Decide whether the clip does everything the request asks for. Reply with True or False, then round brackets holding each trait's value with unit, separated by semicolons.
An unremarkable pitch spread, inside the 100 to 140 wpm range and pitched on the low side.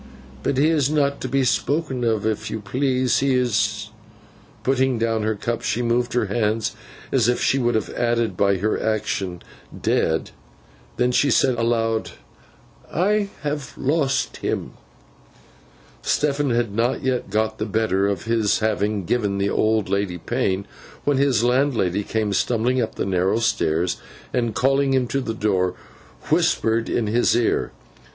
False (3.6 semitones; 155 wpm; 115 Hz)